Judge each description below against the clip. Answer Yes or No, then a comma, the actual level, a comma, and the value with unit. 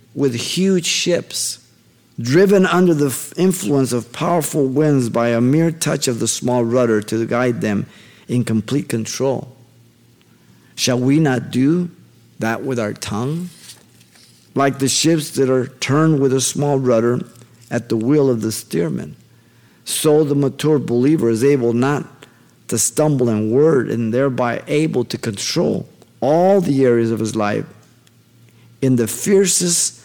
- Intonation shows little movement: No, average, 4.1 semitones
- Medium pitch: No, low, 130 Hz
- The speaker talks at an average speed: Yes, average, 145 wpm